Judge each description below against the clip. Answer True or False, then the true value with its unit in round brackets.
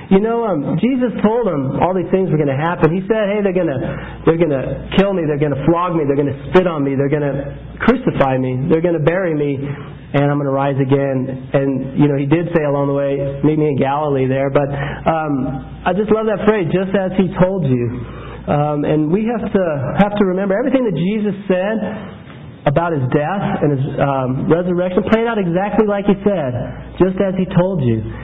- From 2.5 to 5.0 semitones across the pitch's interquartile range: False (5.6 semitones)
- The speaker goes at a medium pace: False (225 wpm)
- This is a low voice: False (160 Hz)